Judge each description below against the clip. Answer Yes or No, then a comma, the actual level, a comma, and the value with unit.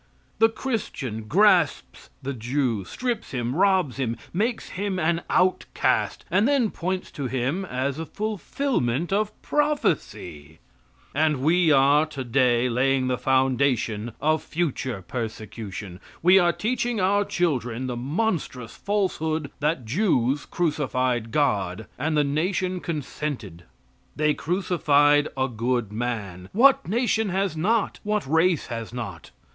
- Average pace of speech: No, slow, 125 wpm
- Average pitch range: No, wide, 7.2 semitones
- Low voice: No, medium, 145 Hz